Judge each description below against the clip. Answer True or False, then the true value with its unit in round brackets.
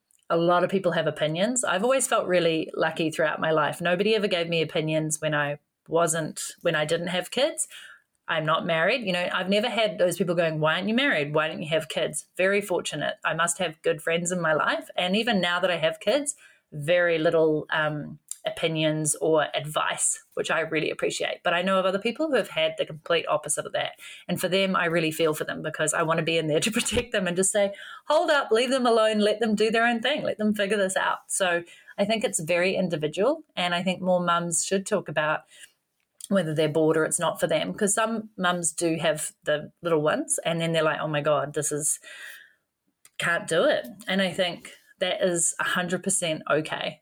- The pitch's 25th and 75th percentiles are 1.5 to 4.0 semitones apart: False (4.8 semitones)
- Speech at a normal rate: False (220 wpm)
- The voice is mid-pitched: True (180 Hz)